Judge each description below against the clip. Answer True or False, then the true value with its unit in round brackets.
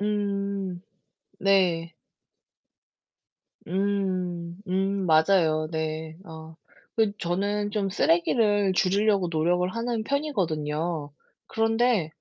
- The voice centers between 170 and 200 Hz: True (190 Hz)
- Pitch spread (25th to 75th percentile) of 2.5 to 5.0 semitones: True (3.7 semitones)